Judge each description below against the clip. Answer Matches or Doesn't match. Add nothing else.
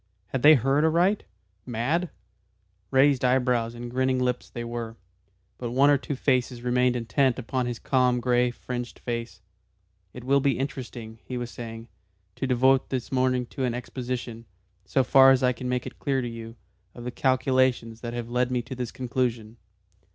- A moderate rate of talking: Matches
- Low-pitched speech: Matches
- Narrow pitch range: Matches